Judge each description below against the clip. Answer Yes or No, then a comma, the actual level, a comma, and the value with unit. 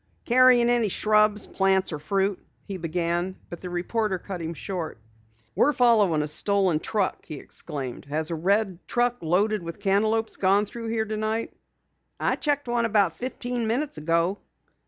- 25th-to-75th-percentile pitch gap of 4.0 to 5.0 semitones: Yes, average, 4.6 semitones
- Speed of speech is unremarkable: Yes, average, 155 wpm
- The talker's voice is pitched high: Yes, high, 200 Hz